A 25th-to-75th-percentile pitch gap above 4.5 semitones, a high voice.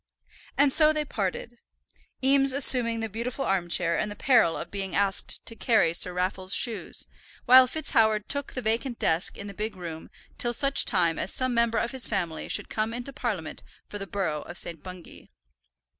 Yes: average, 5.2 semitones; high, 220 Hz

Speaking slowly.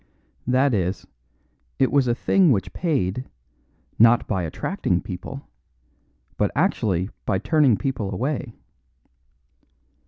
Yes: slow, 105 wpm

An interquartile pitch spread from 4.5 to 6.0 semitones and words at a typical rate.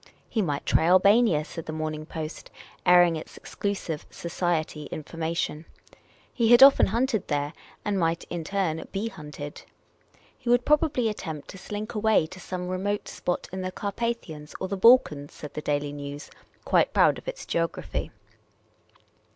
Yes: average, 5.1 semitones; average, 155 wpm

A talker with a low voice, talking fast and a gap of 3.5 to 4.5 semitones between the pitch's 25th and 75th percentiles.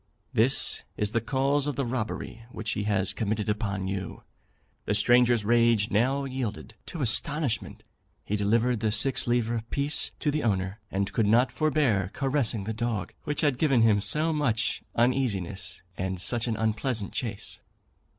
No: low, 115 Hz; average, 160 wpm; average, 4.1 semitones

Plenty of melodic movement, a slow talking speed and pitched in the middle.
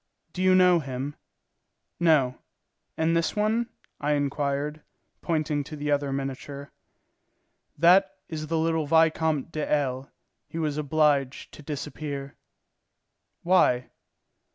No: narrow, 2.6 semitones; slow, 115 wpm; medium, 150 Hz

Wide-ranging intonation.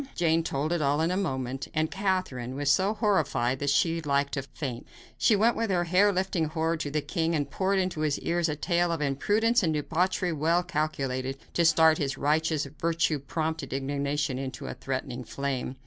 No: average, 3.8 semitones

